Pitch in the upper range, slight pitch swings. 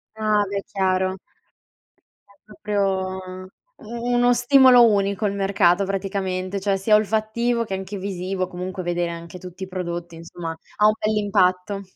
Yes: high, 195 Hz; narrow, 2.3 semitones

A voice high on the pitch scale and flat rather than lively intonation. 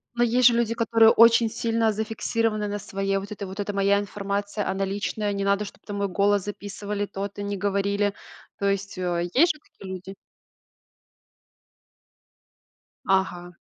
Yes: high, 205 Hz; narrow, 1.8 semitones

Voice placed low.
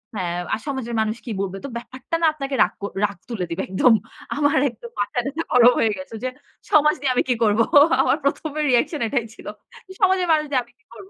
No: high, 245 Hz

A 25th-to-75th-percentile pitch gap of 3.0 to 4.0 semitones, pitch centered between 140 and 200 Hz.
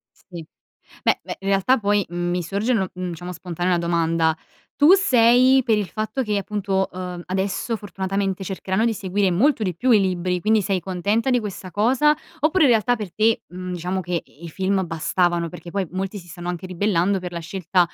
Yes: average, 3.3 semitones; high, 190 Hz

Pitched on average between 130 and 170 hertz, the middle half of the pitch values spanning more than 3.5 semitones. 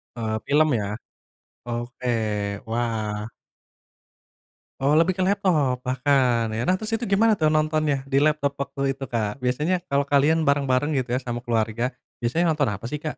Yes: medium, 140 Hz; average, 4.3 semitones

